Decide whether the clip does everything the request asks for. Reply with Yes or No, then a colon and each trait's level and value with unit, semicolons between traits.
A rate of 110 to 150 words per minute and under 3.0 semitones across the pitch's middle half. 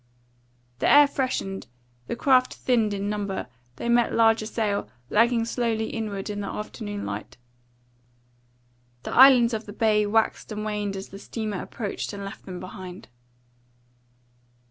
Yes: average, 145 wpm; narrow, 2.4 semitones